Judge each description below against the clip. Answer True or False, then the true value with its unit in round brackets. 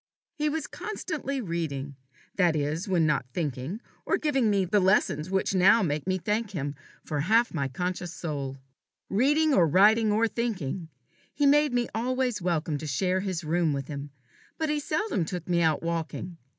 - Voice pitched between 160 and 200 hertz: True (185 Hz)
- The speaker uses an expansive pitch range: True (6.6 semitones)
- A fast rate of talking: False (175 wpm)